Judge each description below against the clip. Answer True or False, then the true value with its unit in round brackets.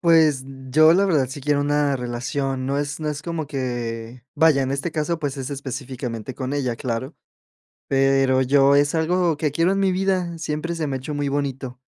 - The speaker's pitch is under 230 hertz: True (140 Hz)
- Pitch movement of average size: True (3.1 semitones)